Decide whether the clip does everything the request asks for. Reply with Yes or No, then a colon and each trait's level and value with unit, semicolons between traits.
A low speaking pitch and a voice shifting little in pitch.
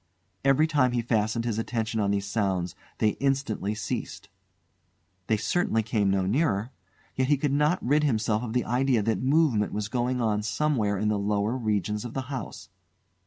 No: low, 115 Hz; average, 3.9 semitones